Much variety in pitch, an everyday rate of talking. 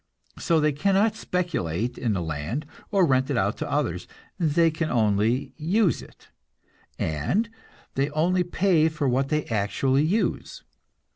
Yes: wide, 6.3 semitones; average, 145 wpm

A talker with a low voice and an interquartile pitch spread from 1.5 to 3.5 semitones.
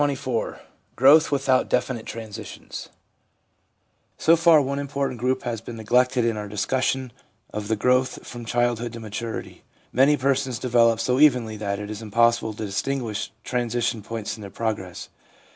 Yes: low, 120 Hz; average, 2.9 semitones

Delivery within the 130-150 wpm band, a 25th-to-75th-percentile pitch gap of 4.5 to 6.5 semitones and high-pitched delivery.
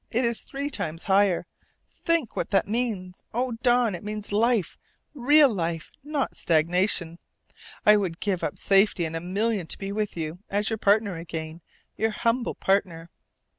No: average, 165 wpm; average, 5.0 semitones; high, 200 Hz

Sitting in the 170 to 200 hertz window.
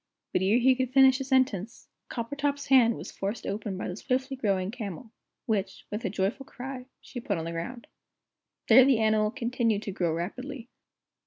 No: high, 230 Hz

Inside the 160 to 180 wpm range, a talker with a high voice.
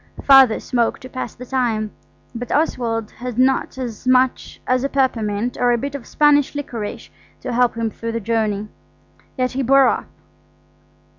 Yes: average, 165 wpm; very high, 250 Hz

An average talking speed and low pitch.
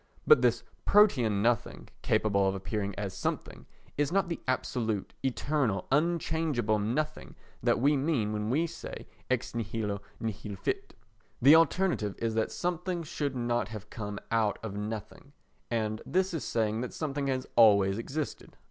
Yes: average, 150 wpm; low, 120 Hz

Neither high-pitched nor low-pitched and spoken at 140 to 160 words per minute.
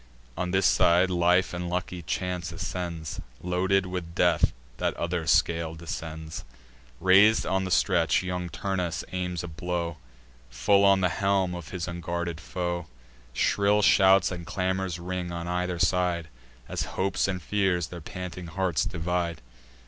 No: very low, 90 Hz; average, 145 wpm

